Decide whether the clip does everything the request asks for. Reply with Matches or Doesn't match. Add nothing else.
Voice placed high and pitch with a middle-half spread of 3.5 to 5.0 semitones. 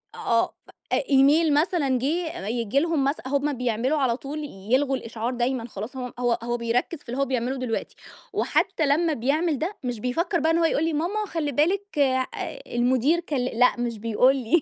Matches